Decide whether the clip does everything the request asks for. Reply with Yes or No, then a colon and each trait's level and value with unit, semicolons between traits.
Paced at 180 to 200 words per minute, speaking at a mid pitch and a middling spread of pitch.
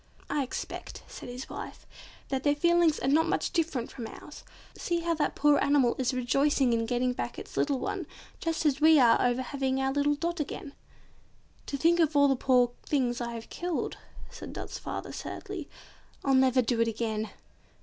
No: average, 190 wpm; very high, 270 Hz; average, 3.4 semitones